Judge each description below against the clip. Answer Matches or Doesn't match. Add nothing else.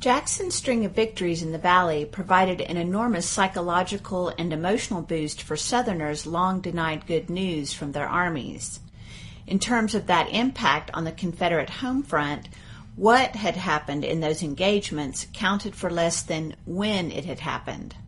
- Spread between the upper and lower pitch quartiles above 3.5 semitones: Matches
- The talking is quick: Doesn't match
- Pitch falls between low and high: Matches